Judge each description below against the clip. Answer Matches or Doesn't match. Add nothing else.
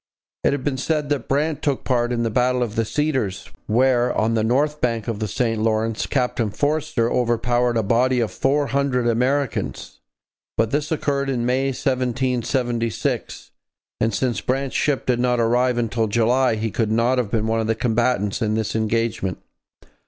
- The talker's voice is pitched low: Matches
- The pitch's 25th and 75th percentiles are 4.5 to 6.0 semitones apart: Doesn't match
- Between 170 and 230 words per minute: Matches